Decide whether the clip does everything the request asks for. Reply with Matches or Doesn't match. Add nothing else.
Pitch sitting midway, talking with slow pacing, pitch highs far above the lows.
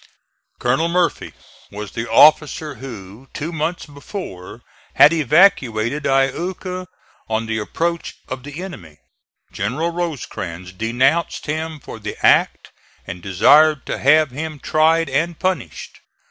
Matches